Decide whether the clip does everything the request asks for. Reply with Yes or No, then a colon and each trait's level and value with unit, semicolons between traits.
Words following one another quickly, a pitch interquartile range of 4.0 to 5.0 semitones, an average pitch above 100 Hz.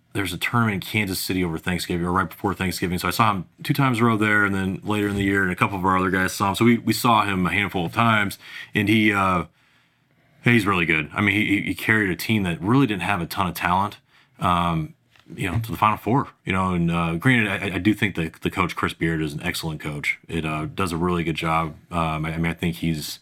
No: fast, 270 wpm; average, 4.4 semitones; very low, 95 Hz